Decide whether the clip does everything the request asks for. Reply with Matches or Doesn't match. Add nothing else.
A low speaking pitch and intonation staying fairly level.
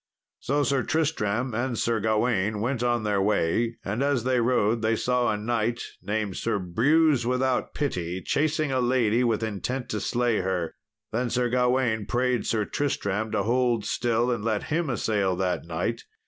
Doesn't match